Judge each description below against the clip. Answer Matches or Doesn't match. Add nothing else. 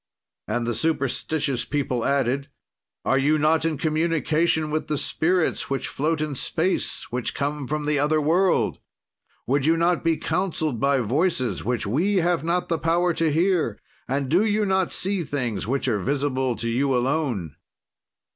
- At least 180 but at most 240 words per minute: Doesn't match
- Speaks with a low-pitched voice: Doesn't match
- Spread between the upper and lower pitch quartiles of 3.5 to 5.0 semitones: Matches